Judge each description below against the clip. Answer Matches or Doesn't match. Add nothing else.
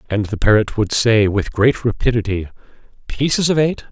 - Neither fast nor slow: Matches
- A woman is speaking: Doesn't match